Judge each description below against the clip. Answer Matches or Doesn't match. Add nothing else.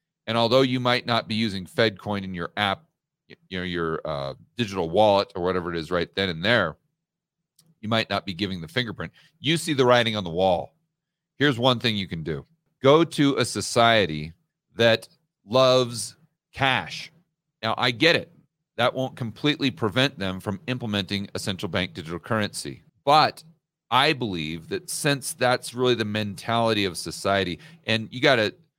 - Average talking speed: Matches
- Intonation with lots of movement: Matches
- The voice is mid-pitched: Doesn't match